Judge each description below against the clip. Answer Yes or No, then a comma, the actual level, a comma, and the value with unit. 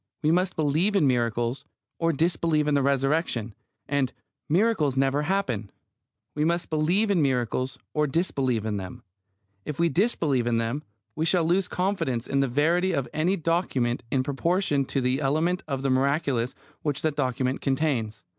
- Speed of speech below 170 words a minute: Yes, average, 155 wpm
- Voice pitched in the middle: Yes, medium, 145 Hz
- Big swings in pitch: No, average, 4.4 semitones